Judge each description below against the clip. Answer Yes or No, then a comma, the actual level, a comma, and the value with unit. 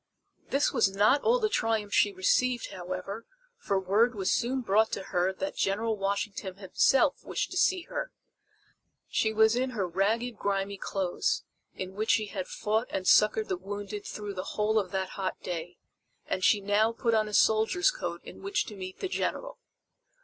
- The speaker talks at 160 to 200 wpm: Yes, average, 180 wpm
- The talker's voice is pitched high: Yes, high, 210 Hz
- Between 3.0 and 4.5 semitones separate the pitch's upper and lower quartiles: Yes, average, 3.4 semitones